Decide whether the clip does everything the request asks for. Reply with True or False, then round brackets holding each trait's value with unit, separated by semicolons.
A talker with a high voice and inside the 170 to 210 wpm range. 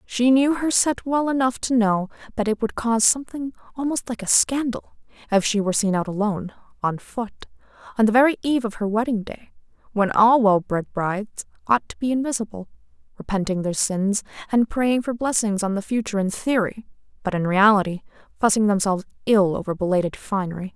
True (220 Hz; 180 wpm)